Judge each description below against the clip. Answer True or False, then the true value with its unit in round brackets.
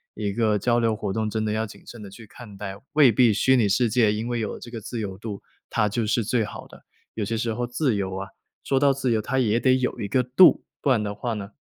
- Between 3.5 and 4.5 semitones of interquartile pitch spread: False (2.8 semitones)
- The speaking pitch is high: False (110 Hz)